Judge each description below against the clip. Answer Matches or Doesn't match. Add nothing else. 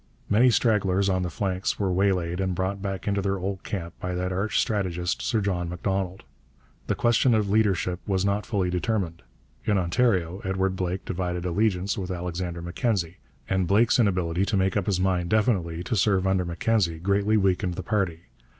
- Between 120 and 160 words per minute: Doesn't match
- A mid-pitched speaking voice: Doesn't match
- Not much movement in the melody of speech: Matches